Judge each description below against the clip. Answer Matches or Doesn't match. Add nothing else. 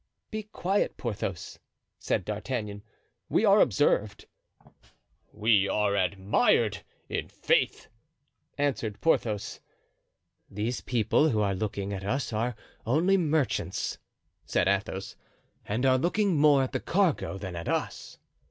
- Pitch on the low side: Matches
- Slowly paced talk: Matches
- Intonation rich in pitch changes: Matches